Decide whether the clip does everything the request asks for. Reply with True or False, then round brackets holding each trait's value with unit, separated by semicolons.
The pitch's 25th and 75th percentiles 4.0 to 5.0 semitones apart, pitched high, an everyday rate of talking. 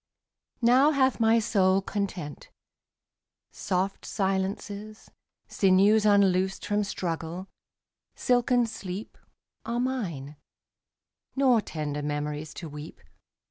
False (4.5 semitones; 195 Hz; 95 wpm)